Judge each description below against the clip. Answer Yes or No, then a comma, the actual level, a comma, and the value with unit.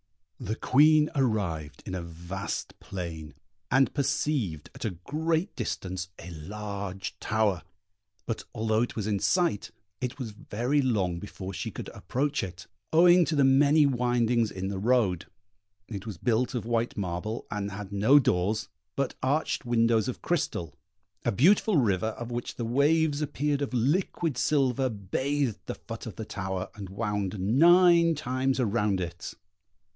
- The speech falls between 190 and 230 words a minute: No, average, 155 wpm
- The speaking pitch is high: No, low, 115 Hz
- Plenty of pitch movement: Yes, wide, 6.1 semitones